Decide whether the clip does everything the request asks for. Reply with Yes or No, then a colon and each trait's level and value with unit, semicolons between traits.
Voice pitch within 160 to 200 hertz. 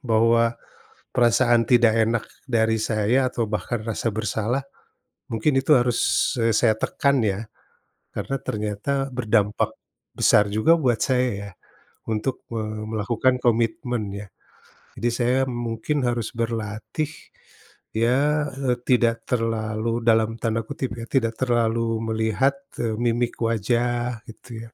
No: low, 115 Hz